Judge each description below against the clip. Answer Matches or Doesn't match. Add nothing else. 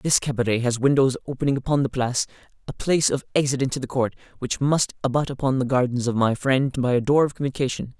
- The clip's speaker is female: Doesn't match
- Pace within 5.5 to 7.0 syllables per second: Matches